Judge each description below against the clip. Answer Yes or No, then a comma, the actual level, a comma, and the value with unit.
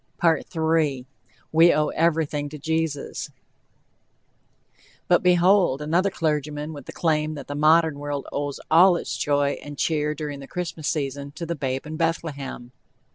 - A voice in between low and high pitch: Yes, medium, 150 Hz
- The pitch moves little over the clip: Yes, narrow, 2.3 semitones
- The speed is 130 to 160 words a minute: Yes, average, 140 wpm